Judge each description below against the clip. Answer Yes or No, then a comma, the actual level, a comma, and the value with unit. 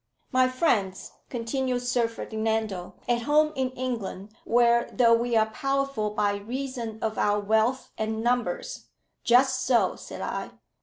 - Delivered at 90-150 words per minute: Yes, average, 145 wpm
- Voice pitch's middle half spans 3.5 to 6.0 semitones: No, average, 2.8 semitones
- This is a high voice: Yes, high, 235 Hz